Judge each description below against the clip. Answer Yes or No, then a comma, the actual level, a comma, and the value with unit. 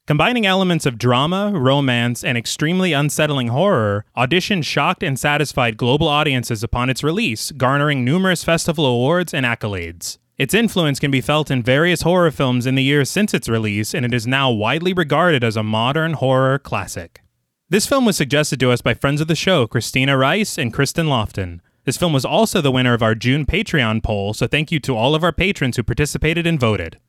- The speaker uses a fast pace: No, average, 195 wpm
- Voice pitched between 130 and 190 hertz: Yes, medium, 140 Hz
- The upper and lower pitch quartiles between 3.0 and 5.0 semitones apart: No, wide, 5.4 semitones